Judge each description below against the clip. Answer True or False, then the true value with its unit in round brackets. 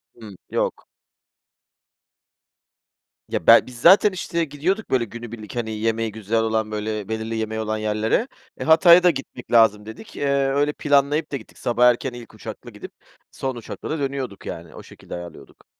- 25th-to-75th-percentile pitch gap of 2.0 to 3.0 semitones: False (4.7 semitones)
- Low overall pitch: True (120 Hz)